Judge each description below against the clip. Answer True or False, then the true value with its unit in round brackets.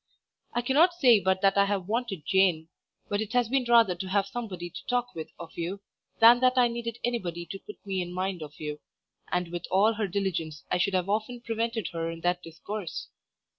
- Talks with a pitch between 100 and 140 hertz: False (195 Hz)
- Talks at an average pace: False (210 wpm)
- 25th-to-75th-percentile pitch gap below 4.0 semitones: False (4.8 semitones)